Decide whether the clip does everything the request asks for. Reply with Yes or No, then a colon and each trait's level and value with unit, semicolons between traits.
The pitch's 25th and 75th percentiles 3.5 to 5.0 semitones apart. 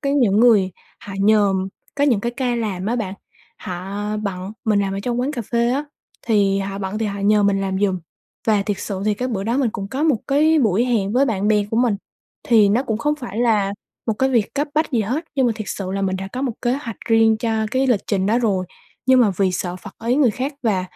Yes: average, 3.9 semitones